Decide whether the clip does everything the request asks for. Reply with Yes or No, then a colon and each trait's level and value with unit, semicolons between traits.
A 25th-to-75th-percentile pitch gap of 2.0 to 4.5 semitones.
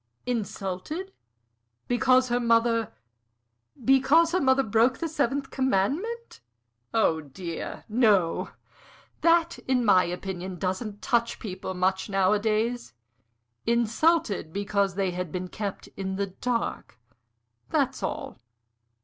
No: wide, 5.4 semitones